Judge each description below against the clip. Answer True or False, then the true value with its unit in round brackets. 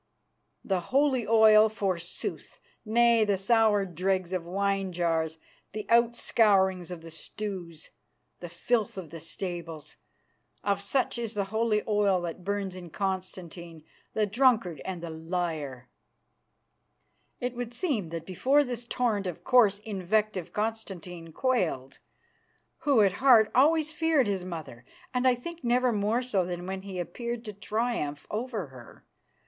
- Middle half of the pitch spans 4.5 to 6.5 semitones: True (4.9 semitones)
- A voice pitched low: False (200 Hz)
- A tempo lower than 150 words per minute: True (140 wpm)